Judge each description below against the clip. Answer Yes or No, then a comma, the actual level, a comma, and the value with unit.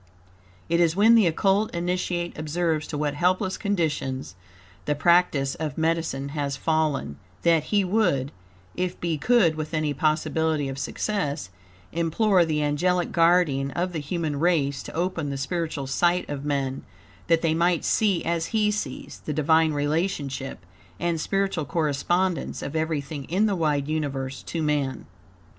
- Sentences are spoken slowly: No, average, 150 wpm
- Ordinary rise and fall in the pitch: Yes, average, 3.3 semitones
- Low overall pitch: No, medium, 160 Hz